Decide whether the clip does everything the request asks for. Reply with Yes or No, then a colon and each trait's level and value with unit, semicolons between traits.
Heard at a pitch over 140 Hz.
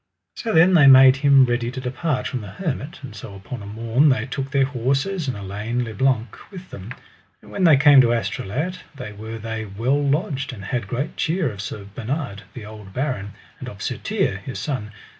No: low, 125 Hz